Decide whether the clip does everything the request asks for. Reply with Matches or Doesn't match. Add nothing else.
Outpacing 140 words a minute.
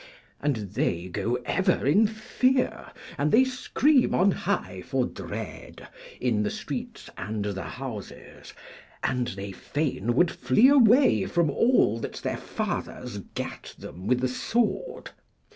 Doesn't match